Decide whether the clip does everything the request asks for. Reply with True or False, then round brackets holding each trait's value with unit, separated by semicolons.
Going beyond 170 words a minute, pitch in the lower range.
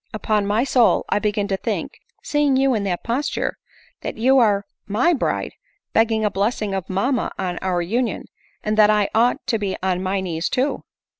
False (190 wpm; 210 Hz)